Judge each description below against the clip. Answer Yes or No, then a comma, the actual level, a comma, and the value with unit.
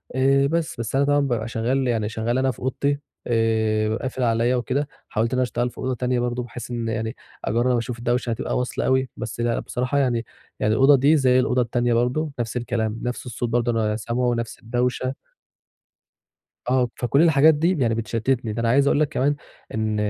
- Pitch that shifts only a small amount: Yes, narrow, 2.3 semitones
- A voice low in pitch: Yes, low, 125 Hz